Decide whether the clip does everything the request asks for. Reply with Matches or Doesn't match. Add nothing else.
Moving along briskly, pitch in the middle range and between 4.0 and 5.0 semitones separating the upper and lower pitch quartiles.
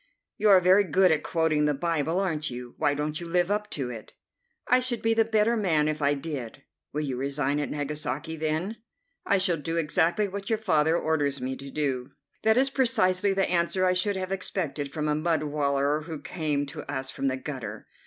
Matches